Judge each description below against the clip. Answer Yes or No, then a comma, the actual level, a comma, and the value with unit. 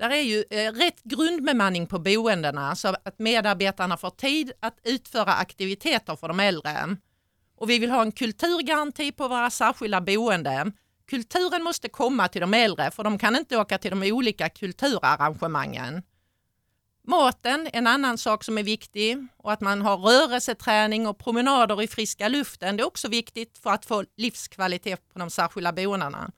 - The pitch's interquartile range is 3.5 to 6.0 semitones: Yes, average, 4.1 semitones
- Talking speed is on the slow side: No, average, 165 wpm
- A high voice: Yes, high, 215 Hz